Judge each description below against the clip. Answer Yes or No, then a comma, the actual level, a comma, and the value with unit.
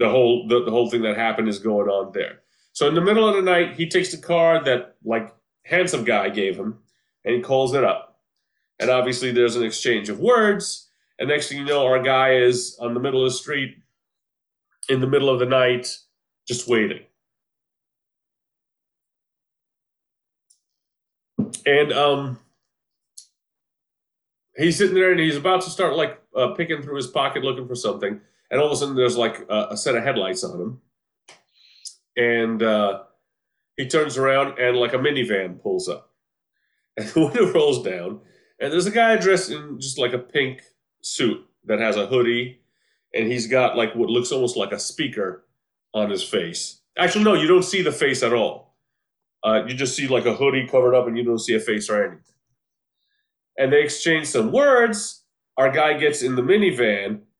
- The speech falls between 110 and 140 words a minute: No, average, 185 wpm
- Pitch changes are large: Yes, wide, 6.7 semitones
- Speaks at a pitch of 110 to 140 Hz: Yes, low, 135 Hz